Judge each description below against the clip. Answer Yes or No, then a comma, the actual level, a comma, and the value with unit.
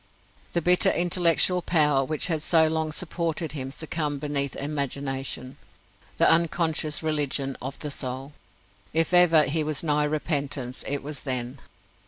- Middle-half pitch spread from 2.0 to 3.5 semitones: Yes, average, 2.7 semitones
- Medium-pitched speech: Yes, medium, 150 Hz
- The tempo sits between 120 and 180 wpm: Yes, average, 140 wpm